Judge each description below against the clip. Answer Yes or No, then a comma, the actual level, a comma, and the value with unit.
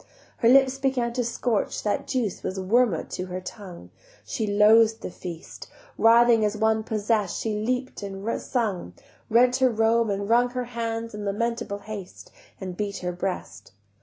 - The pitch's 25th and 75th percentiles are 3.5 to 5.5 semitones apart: No, average, 2.9 semitones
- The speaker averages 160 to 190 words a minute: Yes, average, 165 wpm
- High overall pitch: Yes, high, 220 Hz